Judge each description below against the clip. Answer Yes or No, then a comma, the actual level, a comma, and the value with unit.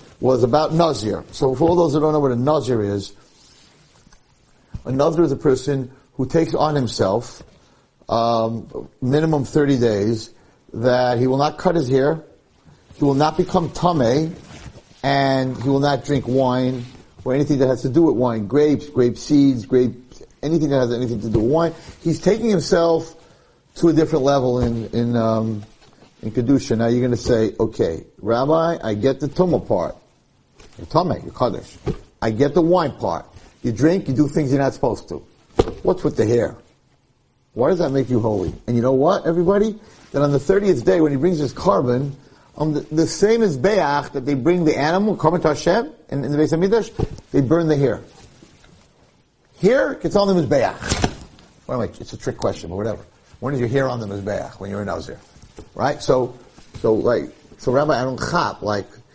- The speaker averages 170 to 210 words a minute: Yes, average, 190 wpm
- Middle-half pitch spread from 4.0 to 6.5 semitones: Yes, average, 4.8 semitones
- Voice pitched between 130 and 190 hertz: Yes, medium, 140 Hz